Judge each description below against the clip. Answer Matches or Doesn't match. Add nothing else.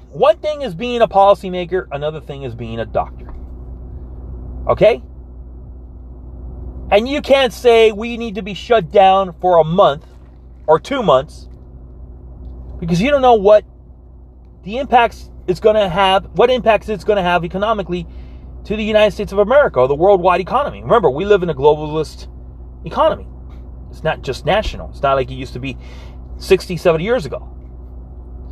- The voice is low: Doesn't match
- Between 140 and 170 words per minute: Matches